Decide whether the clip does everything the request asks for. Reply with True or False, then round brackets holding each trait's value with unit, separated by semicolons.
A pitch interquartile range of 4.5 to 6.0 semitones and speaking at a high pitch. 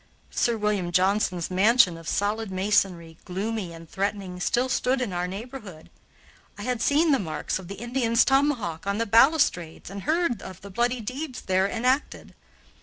True (5.0 semitones; 210 Hz)